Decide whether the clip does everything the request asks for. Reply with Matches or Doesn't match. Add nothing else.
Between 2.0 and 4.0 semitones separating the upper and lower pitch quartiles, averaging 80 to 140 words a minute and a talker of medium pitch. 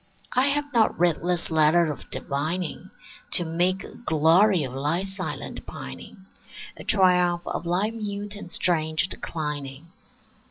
Matches